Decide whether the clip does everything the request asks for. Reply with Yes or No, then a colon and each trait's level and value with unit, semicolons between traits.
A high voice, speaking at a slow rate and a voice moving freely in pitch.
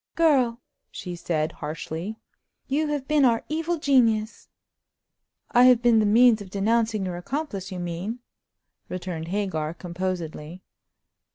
Yes: high, 210 Hz; slow, 125 wpm; wide, 5.9 semitones